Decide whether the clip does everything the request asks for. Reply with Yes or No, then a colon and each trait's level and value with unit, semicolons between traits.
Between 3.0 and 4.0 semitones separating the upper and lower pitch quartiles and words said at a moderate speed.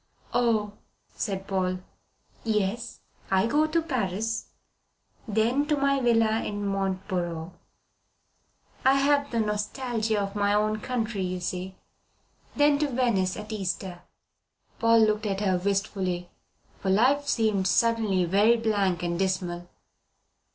No: average, 3.5 semitones; slow, 125 wpm